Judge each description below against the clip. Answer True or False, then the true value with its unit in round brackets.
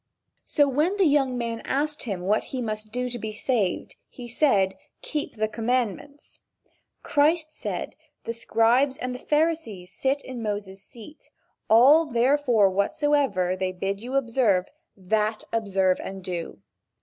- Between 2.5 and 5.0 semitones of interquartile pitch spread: False (5.5 semitones)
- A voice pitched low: False (235 Hz)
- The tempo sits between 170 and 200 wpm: False (145 wpm)